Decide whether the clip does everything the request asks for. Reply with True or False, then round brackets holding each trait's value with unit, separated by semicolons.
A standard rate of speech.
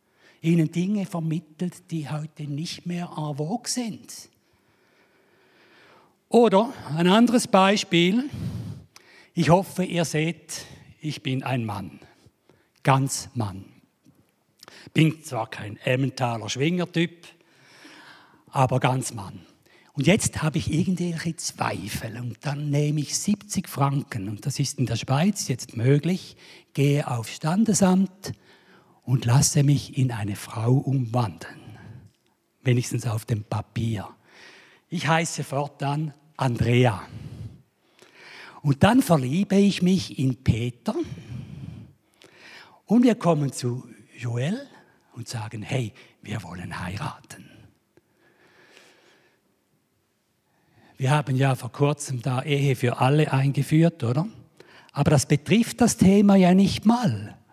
False (110 wpm)